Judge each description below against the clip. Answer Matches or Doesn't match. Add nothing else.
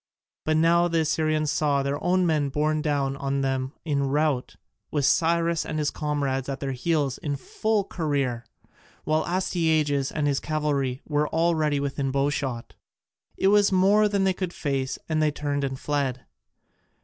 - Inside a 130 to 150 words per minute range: Doesn't match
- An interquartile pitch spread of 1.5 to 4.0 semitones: Matches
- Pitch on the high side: Doesn't match